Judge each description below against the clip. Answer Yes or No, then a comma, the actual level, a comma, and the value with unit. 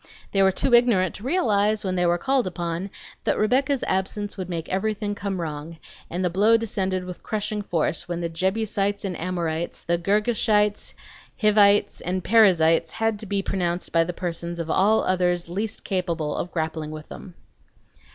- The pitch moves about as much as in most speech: Yes, average, 3.4 semitones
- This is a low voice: No, high, 190 Hz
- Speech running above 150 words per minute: Yes, average, 170 wpm